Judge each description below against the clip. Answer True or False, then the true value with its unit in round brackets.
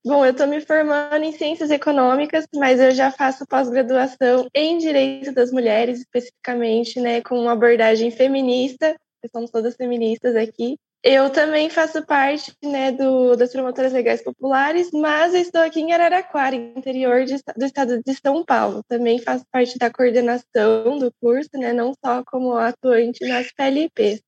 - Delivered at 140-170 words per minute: True (160 wpm)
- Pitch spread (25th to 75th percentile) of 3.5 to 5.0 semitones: False (2.8 semitones)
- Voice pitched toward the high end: True (260 Hz)